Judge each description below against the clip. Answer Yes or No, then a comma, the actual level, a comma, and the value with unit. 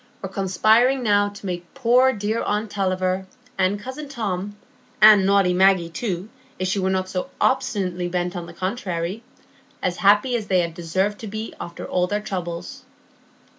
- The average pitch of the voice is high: Yes, high, 195 Hz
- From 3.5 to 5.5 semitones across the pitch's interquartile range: No, average, 2.9 semitones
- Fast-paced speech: No, average, 160 wpm